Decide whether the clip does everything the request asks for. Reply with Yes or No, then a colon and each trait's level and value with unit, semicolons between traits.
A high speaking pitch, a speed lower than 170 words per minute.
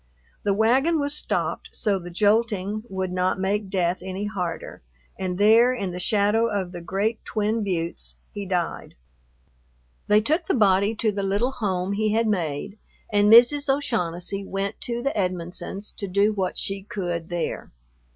Yes: high, 200 Hz; average, 160 wpm